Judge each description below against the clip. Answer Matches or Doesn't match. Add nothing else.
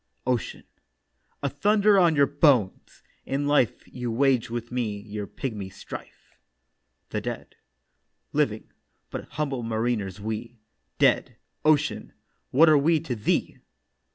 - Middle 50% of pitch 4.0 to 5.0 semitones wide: Matches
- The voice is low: Matches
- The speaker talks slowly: Matches